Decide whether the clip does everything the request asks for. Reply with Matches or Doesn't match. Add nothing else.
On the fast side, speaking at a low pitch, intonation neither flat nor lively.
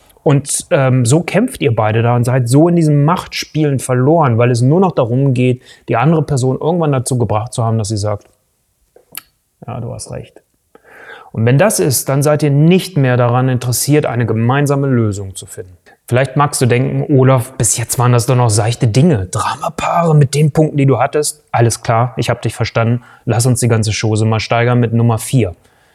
Matches